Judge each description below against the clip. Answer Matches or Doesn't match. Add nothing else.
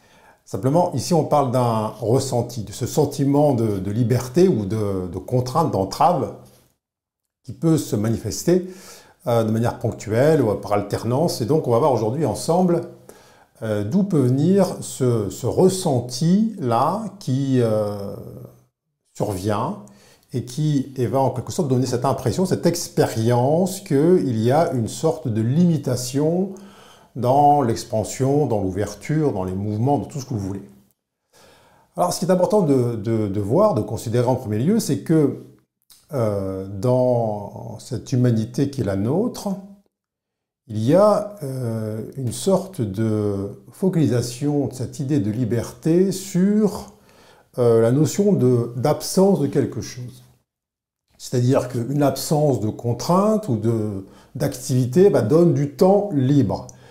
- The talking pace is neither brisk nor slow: Doesn't match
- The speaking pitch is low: Matches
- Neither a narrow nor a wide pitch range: Doesn't match